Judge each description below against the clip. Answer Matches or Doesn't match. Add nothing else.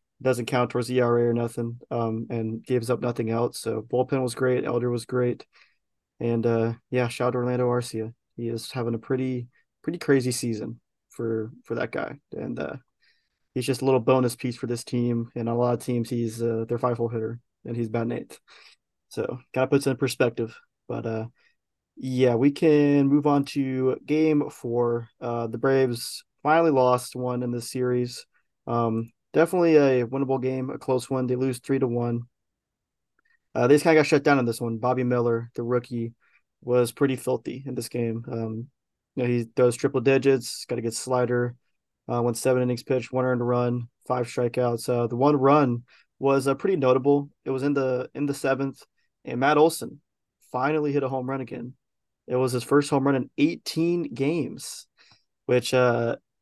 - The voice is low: Matches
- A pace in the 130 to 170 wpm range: Doesn't match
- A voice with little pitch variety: Matches